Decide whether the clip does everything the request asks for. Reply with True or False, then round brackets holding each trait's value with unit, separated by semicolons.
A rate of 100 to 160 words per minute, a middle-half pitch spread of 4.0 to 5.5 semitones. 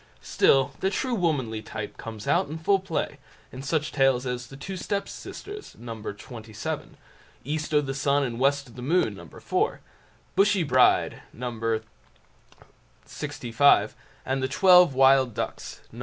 True (155 wpm; 4.9 semitones)